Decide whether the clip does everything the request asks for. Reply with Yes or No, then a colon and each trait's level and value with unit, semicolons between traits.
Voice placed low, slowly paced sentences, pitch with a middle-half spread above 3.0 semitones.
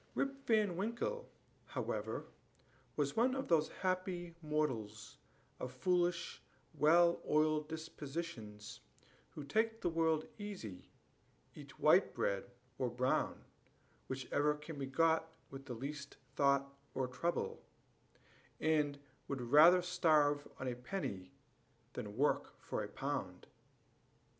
No: medium, 150 Hz; slow, 115 wpm; average, 4.6 semitones